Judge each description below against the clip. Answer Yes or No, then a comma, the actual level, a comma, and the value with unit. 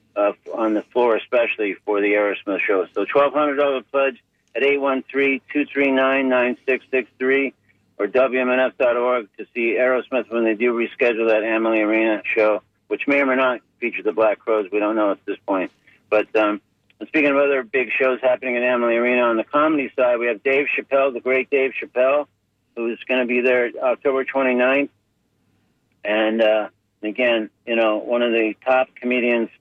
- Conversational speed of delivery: Yes, average, 165 wpm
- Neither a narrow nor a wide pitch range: Yes, average, 3.2 semitones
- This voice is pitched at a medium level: No, low, 125 Hz